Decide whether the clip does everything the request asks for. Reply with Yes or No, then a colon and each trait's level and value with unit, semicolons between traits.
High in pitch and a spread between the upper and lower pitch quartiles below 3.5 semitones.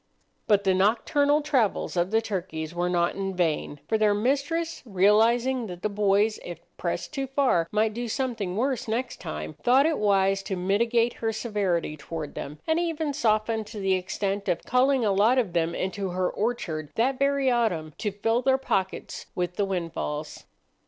No: high, 210 Hz; average, 5.0 semitones